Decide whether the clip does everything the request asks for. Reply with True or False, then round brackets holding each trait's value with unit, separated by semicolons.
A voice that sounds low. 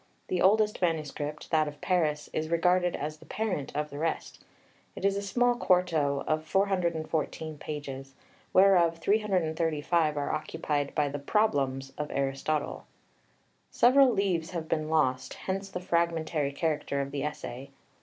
False (160 Hz)